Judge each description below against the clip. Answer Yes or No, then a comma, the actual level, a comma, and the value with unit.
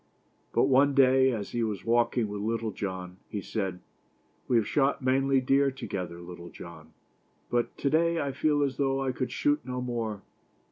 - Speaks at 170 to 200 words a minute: Yes, average, 180 wpm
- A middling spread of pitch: Yes, average, 4.8 semitones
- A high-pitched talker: No, low, 125 Hz